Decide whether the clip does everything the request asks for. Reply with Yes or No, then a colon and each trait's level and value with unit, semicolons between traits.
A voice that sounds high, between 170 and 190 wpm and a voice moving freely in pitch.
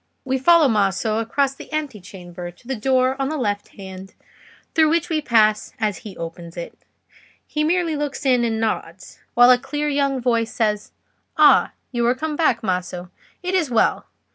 Yes: high, 240 Hz; average, 180 wpm; wide, 5.8 semitones